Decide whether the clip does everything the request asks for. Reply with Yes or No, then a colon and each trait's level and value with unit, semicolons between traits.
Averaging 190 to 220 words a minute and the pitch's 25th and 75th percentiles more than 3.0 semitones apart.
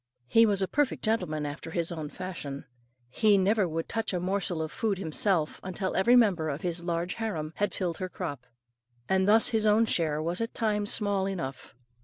Yes: average, 195 wpm; average, 4.3 semitones